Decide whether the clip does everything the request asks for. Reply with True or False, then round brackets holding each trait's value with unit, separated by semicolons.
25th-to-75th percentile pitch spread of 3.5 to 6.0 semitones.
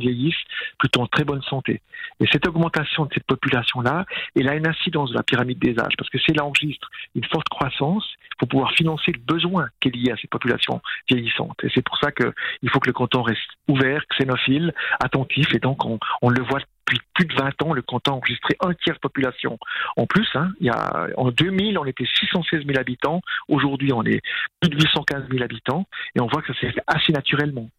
True (4.1 semitones)